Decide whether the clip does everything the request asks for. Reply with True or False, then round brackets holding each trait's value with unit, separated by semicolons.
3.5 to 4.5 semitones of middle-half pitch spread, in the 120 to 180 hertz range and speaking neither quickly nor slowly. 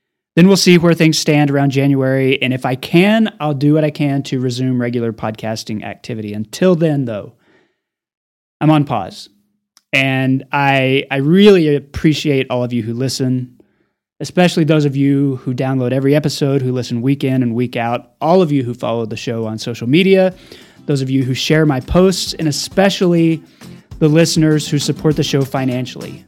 True (3.8 semitones; 140 Hz; 180 wpm)